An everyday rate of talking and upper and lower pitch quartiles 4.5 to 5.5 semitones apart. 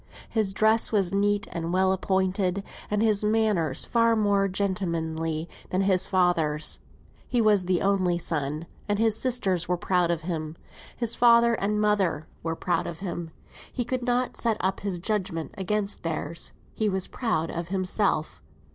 No: average, 160 wpm; average, 3.7 semitones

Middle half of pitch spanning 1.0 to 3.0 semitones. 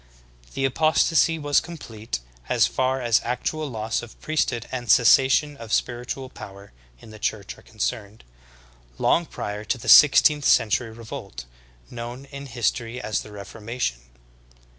No: average, 3.8 semitones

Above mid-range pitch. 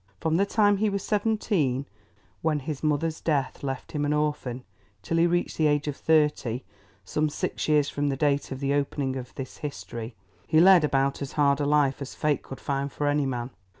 No: medium, 145 Hz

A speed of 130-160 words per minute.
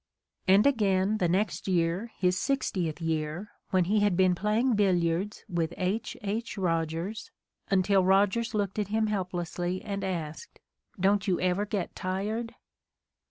Yes: average, 140 wpm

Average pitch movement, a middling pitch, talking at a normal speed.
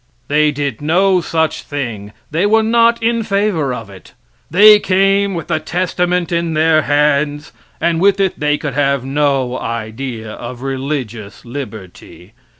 No: wide, 6.1 semitones; medium, 150 Hz; average, 150 wpm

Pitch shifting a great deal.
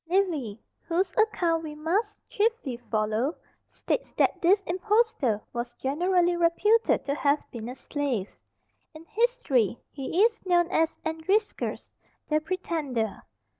Yes: wide, 6.4 semitones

